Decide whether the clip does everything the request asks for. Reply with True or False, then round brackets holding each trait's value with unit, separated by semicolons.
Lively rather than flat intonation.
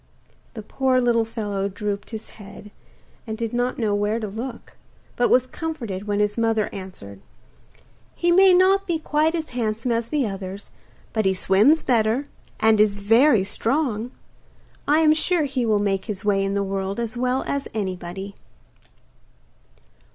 False (4.3 semitones)